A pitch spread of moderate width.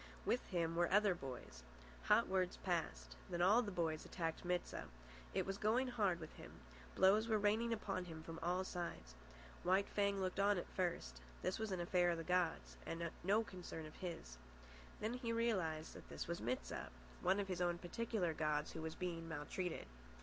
Yes: average, 3.5 semitones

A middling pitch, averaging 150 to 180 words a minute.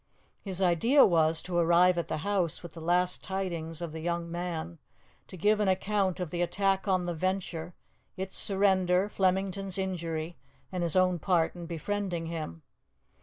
Yes: medium, 180 Hz; average, 170 wpm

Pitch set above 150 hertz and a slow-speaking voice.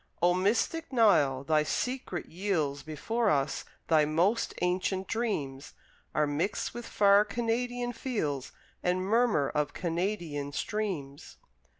Yes: medium, 185 Hz; slow, 115 wpm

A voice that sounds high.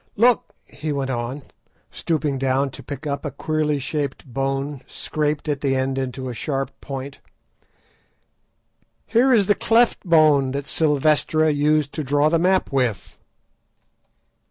No: medium, 145 Hz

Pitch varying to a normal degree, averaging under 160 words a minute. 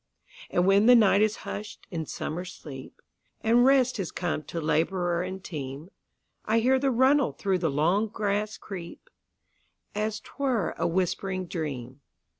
Yes: average, 4.8 semitones; average, 140 wpm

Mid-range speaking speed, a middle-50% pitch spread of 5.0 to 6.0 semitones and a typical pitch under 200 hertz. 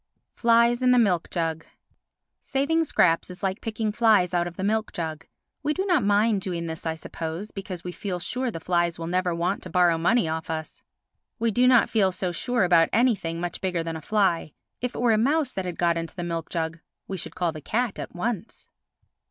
No: fast, 220 wpm; average, 5.3 semitones; medium, 185 Hz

